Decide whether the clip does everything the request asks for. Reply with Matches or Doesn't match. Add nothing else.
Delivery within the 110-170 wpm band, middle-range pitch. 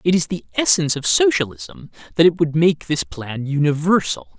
Doesn't match